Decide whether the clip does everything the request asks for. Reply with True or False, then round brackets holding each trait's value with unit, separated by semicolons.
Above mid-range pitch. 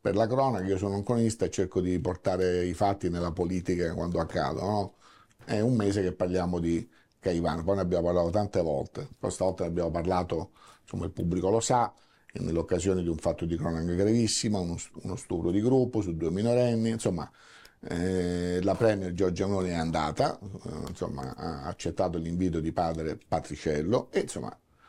False (90 Hz)